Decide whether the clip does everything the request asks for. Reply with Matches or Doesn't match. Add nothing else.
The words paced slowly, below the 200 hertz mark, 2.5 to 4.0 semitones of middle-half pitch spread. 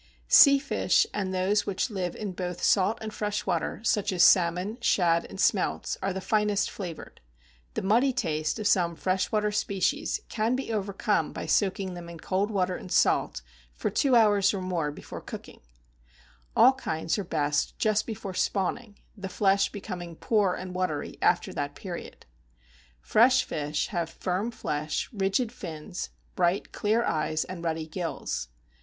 Doesn't match